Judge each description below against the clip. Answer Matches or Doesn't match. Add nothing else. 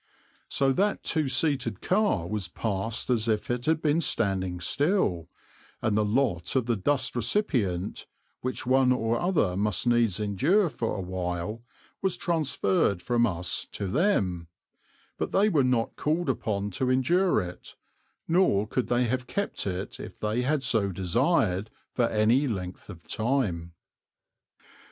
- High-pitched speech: Doesn't match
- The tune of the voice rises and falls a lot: Matches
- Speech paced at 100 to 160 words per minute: Matches